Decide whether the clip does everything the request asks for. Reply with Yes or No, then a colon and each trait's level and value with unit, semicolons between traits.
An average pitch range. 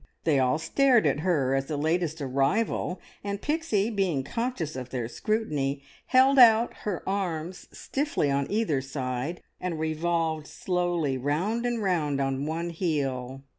No: wide, 6.5 semitones